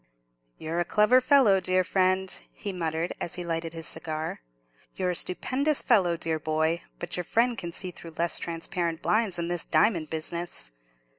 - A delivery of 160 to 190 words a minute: Yes, average, 170 wpm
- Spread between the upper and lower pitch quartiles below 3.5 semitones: Yes, average, 2.8 semitones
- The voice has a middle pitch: Yes, medium, 175 Hz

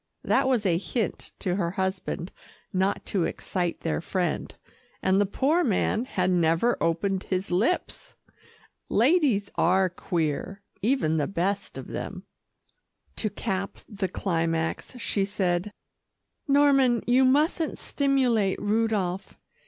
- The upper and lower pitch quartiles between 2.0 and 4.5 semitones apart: No, average, 4.9 semitones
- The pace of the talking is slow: Yes, slow, 120 wpm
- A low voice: No, high, 195 Hz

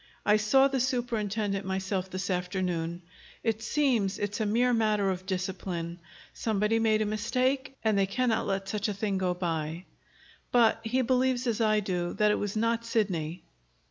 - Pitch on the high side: Yes, high, 210 Hz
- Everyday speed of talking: Yes, average, 170 wpm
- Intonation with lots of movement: No, average, 3.4 semitones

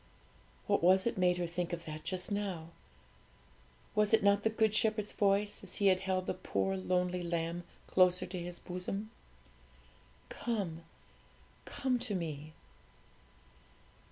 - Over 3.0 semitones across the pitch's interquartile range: No, average, 2.7 semitones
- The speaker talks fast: No, average, 140 wpm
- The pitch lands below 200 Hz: Yes, medium, 185 Hz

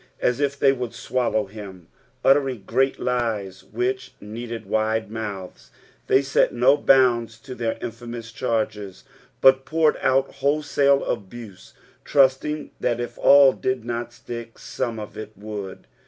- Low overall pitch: Yes, low, 120 Hz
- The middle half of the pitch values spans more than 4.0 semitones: No, average, 3.5 semitones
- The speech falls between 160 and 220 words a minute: No, average, 140 wpm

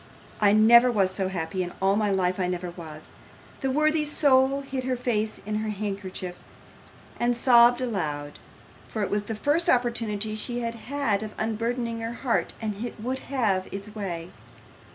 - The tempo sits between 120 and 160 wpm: No, average, 175 wpm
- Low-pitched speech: No, high, 220 Hz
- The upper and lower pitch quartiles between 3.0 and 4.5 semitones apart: Yes, average, 3.9 semitones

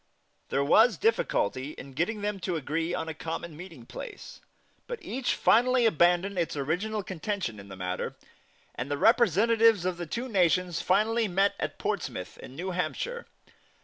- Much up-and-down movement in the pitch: Yes, wide, 5.7 semitones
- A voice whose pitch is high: No, medium, 180 Hz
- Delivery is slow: No, average, 160 wpm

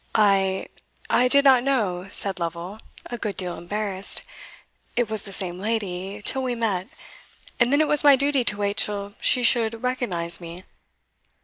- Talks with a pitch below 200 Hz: No, high, 210 Hz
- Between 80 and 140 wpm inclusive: No, average, 170 wpm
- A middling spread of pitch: Yes, average, 4.6 semitones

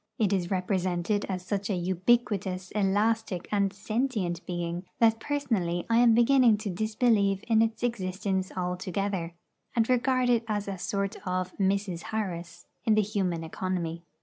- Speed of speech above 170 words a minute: No, average, 150 wpm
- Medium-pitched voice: No, high, 200 Hz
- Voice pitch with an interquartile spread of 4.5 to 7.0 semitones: No, average, 3.4 semitones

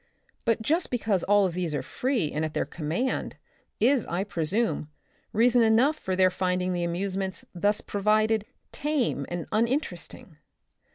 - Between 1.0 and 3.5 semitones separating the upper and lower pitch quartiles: No, average, 4.6 semitones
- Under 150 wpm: Yes, average, 140 wpm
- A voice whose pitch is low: No, high, 205 Hz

